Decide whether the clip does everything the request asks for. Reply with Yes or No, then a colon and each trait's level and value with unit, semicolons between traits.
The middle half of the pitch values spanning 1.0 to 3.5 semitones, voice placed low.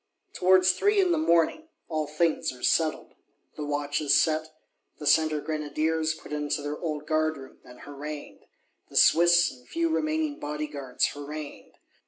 No: narrow, 2.6 semitones; medium, 155 Hz